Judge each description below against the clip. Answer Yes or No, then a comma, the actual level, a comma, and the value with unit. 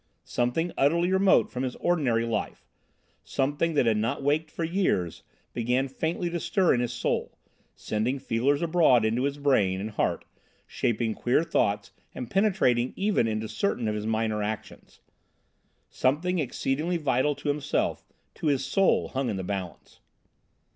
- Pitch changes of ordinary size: No, wide, 6.0 semitones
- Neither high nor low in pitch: No, low, 130 Hz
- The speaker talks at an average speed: Yes, average, 155 wpm